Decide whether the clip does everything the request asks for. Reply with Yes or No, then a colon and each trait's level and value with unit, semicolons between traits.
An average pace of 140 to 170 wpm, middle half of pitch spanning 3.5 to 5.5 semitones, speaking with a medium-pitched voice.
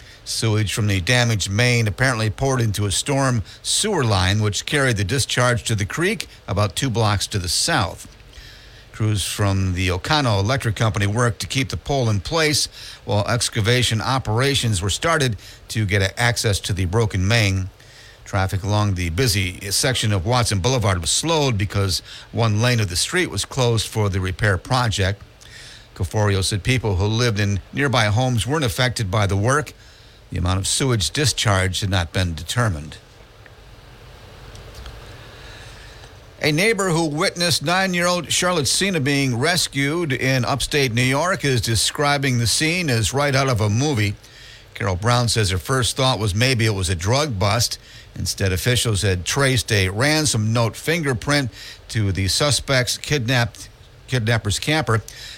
No: average, 160 wpm; average, 4.0 semitones; low, 115 Hz